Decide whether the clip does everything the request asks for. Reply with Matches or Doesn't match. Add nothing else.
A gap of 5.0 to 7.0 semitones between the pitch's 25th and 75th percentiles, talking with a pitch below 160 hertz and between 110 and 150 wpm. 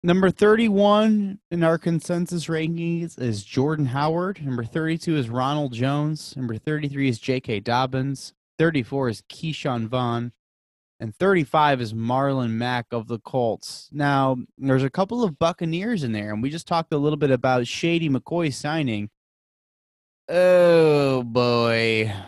Matches